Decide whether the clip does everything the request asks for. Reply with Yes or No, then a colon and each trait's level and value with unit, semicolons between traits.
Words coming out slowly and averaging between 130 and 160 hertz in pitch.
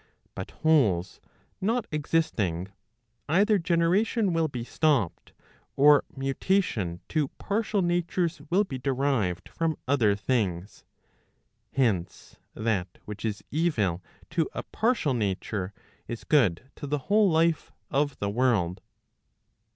Yes: slow, 115 wpm; medium, 140 Hz